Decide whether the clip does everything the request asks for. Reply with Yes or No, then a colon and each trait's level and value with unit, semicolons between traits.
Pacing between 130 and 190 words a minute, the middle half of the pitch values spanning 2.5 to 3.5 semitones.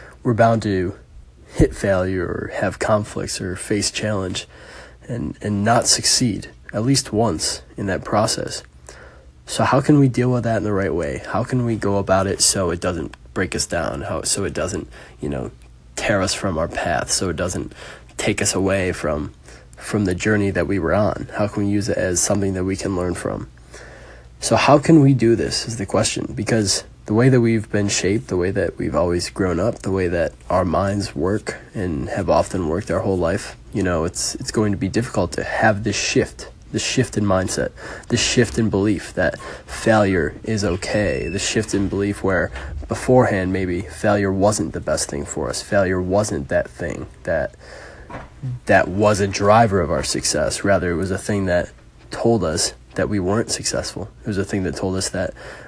No: average, 200 wpm; average, 3.0 semitones